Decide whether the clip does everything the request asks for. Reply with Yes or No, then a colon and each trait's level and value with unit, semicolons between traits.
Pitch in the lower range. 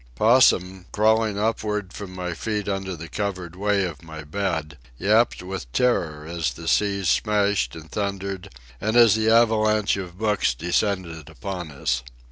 Yes: very low, 95 Hz